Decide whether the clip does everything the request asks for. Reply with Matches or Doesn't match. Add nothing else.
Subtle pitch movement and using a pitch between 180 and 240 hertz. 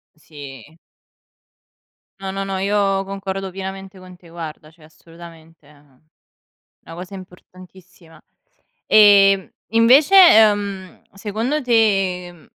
Doesn't match